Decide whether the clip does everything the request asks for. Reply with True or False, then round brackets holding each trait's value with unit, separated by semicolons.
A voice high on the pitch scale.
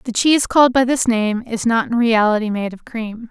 True (230 Hz)